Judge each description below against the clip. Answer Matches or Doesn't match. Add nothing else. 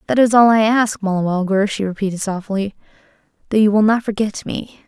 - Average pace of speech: Matches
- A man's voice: Doesn't match